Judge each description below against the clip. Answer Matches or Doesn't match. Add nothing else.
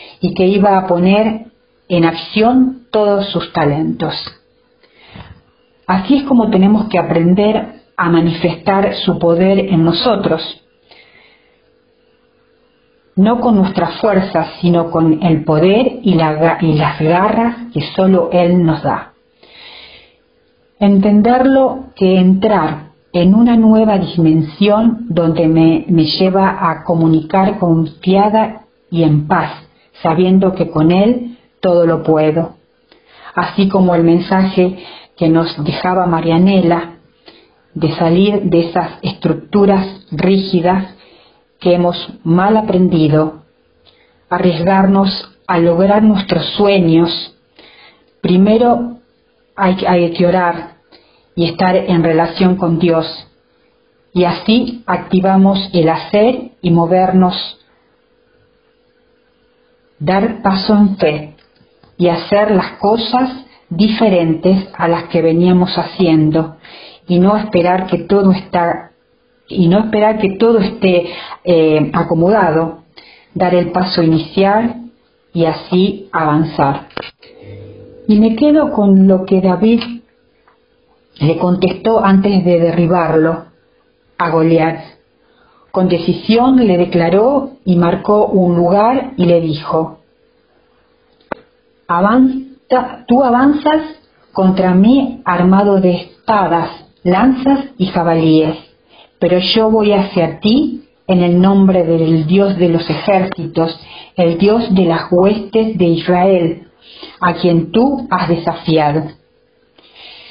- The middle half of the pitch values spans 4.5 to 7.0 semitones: Doesn't match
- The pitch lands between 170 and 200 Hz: Matches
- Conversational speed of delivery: Doesn't match